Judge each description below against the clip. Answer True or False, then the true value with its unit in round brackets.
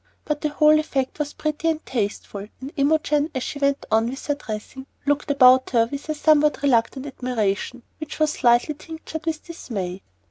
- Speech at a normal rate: True (180 wpm)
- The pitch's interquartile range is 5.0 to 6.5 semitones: False (3.6 semitones)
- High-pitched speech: True (285 Hz)